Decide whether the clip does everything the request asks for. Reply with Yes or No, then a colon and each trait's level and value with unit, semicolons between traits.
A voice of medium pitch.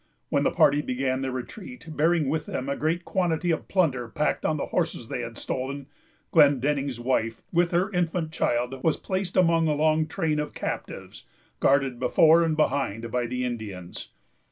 Yes: medium, 150 Hz